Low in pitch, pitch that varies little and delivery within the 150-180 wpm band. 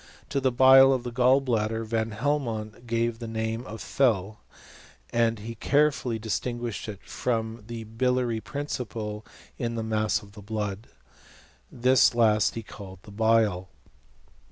Yes: low, 115 Hz; narrow, 2.3 semitones; average, 155 wpm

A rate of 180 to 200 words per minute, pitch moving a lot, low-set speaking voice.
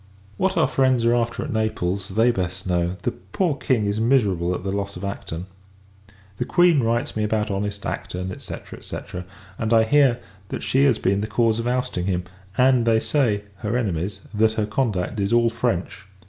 No: average, 190 wpm; average, 3.8 semitones; low, 110 Hz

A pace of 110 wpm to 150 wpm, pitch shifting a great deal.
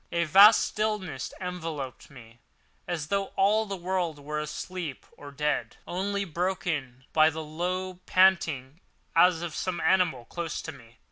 No: average, 140 wpm; average, 4.1 semitones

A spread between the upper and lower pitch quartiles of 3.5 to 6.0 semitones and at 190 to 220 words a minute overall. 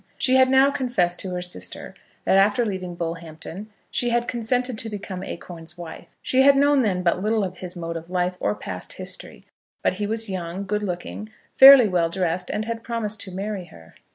Yes: average, 4.6 semitones; average, 200 wpm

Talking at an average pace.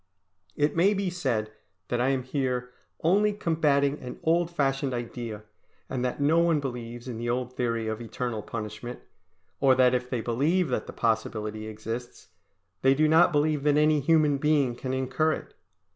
Yes: average, 175 wpm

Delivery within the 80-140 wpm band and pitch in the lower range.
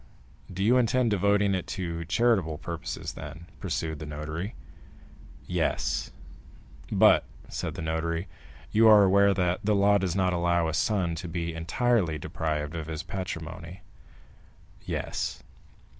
Yes: slow, 135 wpm; very low, 90 Hz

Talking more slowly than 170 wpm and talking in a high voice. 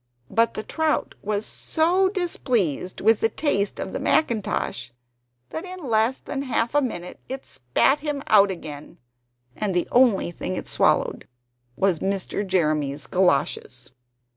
Yes: average, 140 wpm; high, 215 Hz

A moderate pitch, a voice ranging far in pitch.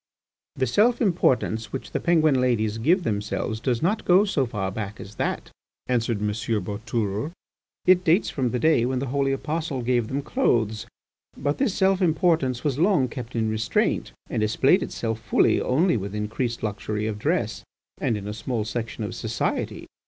No: low, 120 Hz; wide, 5.9 semitones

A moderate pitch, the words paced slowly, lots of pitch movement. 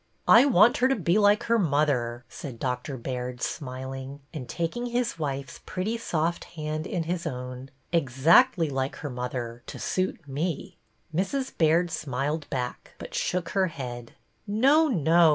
No: medium, 155 Hz; average, 155 wpm; wide, 6.0 semitones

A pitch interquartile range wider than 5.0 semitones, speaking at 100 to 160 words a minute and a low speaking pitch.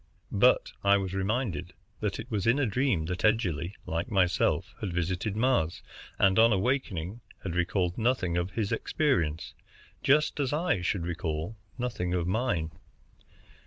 Yes: wide, 5.4 semitones; average, 150 wpm; very low, 95 Hz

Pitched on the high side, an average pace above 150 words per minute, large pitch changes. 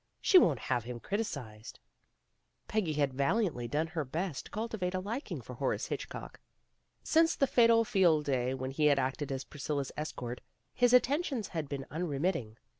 No: medium, 155 Hz; average, 180 wpm; wide, 7.9 semitones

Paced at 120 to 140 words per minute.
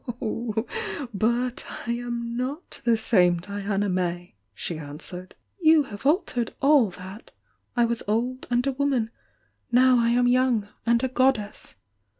No: average, 150 wpm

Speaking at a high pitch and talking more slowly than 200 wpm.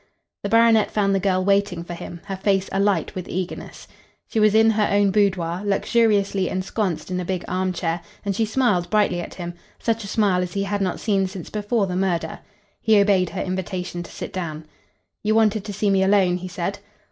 No: high, 195 Hz; fast, 205 wpm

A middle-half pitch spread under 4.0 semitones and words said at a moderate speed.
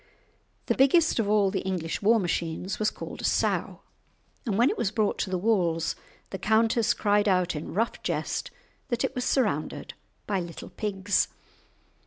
Yes: average, 3.5 semitones; average, 170 wpm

